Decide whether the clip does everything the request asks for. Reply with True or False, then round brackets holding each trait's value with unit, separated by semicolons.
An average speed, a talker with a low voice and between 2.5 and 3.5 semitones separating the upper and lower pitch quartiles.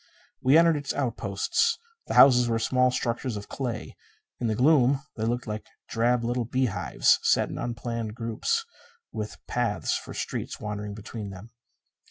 True (155 wpm; 120 Hz; 2.9 semitones)